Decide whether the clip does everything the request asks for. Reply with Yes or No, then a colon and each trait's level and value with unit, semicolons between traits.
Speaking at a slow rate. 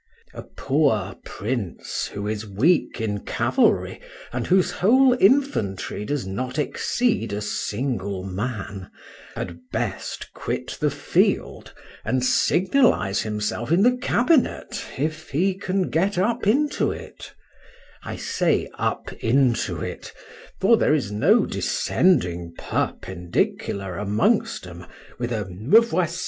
Yes: slow, 115 wpm